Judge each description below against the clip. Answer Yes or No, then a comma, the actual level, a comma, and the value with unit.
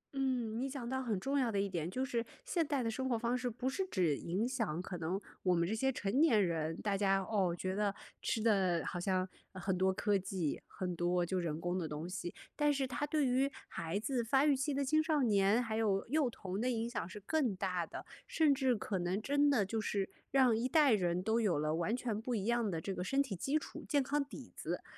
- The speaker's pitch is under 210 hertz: No, high, 220 Hz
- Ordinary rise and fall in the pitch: No, wide, 5.9 semitones